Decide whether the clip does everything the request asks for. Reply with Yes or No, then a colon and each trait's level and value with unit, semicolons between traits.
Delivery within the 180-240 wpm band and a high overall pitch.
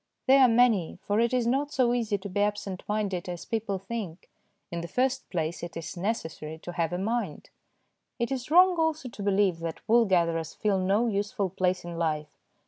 Yes: average, 200 wpm; high, 205 Hz